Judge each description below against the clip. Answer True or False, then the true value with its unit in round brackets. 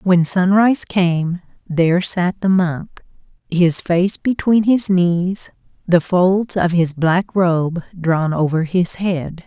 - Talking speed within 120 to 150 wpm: True (140 wpm)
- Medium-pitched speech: True (175 Hz)